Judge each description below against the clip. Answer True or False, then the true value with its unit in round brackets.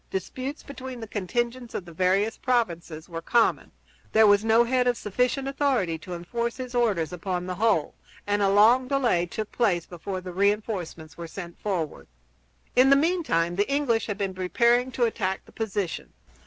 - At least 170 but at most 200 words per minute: True (180 wpm)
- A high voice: True (210 Hz)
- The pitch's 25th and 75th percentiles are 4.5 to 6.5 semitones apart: True (5.2 semitones)